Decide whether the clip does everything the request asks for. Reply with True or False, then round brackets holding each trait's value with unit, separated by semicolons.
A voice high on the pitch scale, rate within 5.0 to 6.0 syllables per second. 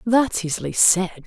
False (195 Hz; 4.4 syllables/s)